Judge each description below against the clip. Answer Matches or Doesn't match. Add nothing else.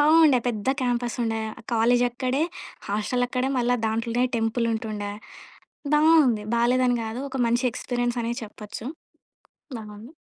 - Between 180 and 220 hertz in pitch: Doesn't match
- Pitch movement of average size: Doesn't match